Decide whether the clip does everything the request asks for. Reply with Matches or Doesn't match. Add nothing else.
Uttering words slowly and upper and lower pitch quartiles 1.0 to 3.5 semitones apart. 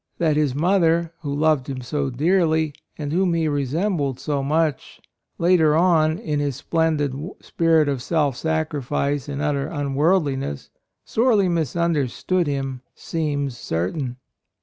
Matches